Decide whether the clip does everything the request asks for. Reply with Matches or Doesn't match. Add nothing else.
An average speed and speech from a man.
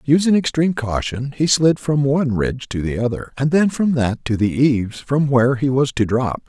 Doesn't match